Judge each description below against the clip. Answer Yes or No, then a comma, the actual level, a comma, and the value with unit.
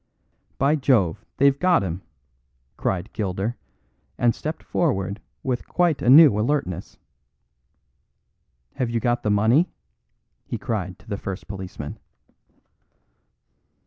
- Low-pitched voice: Yes, low, 110 Hz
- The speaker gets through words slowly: Yes, slow, 110 wpm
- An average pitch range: No, wide, 6.1 semitones